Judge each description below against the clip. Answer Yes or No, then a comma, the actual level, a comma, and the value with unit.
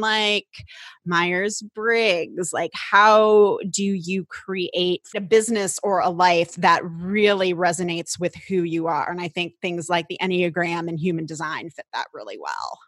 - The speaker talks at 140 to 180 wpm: Yes, average, 160 wpm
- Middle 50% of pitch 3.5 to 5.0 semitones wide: No, average, 2.8 semitones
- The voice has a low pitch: No, medium, 180 Hz